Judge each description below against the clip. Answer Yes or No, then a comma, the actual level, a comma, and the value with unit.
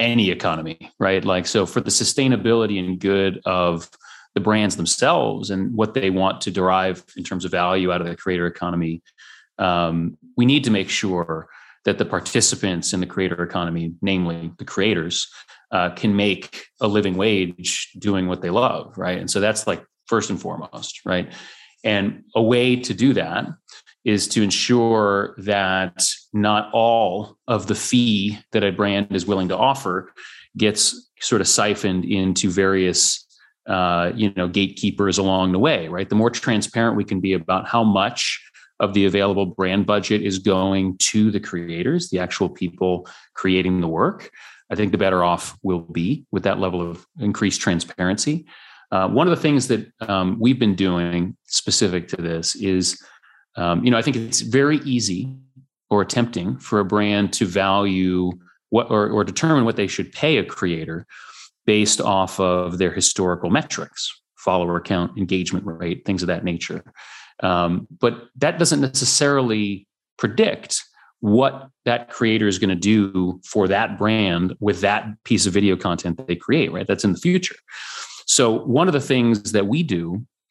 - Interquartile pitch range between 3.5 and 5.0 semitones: No, average, 3.1 semitones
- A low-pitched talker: Yes, low, 100 Hz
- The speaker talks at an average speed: Yes, average, 170 wpm